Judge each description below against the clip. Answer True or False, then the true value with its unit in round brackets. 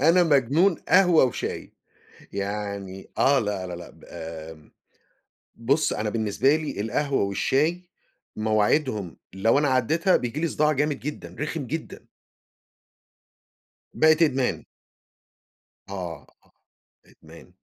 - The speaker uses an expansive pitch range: True (7.2 semitones)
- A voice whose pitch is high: False (130 Hz)